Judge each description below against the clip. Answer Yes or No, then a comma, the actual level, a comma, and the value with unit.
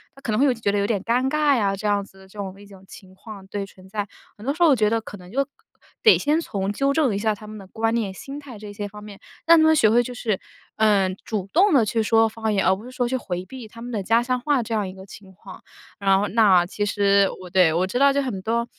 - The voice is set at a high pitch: Yes, high, 215 Hz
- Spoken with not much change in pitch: No, average, 3.8 semitones